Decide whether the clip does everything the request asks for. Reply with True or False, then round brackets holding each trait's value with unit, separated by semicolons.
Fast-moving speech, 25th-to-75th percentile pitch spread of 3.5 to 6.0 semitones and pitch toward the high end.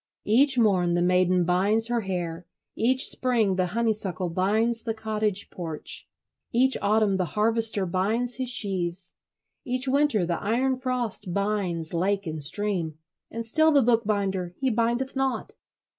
False (145 wpm; 4.5 semitones; 210 Hz)